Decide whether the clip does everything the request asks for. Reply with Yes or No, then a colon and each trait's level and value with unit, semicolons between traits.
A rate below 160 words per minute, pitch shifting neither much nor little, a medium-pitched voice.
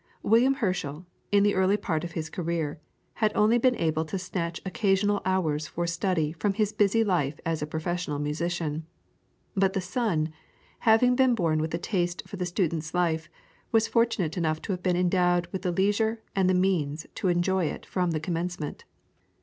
No: average, 180 wpm; average, 3.8 semitones; medium, 180 Hz